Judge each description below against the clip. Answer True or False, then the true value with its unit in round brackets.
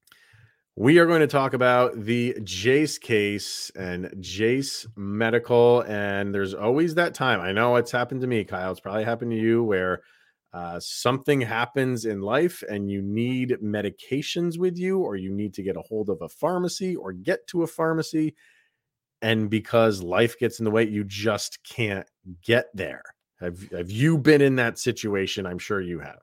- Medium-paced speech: True (180 wpm)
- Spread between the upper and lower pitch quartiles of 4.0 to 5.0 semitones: True (4.5 semitones)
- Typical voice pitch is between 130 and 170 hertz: False (115 Hz)